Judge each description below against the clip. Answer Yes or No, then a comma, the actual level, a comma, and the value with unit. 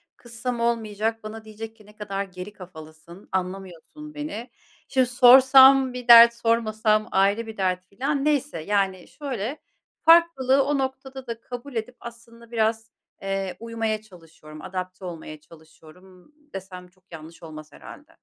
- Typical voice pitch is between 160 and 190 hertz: No, high, 220 Hz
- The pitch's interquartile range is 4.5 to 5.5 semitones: Yes, average, 5.1 semitones